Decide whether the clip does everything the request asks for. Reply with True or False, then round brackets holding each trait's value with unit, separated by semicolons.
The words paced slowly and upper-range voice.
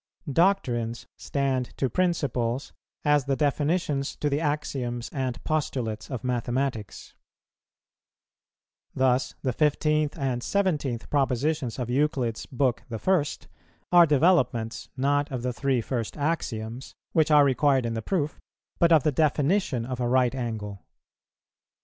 False (125 wpm; 135 Hz)